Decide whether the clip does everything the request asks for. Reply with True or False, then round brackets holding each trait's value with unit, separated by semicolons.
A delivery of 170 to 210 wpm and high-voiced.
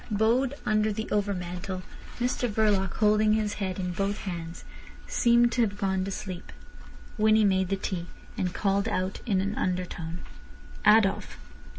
False (150 wpm; 200 Hz)